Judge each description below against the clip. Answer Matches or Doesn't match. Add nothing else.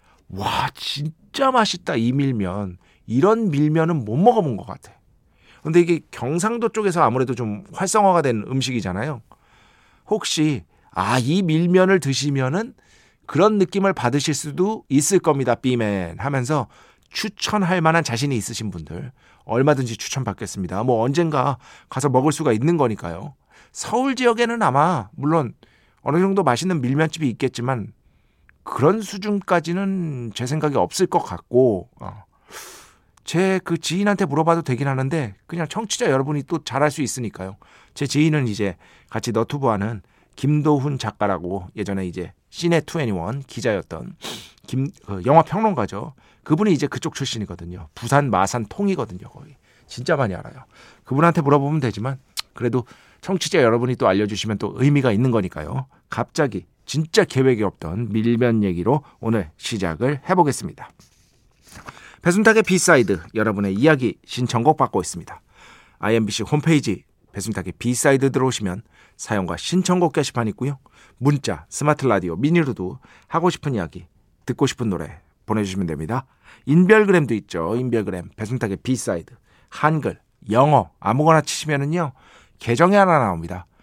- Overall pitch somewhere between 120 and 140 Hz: Matches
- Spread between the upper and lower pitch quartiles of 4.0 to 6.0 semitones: Doesn't match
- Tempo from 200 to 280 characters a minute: Doesn't match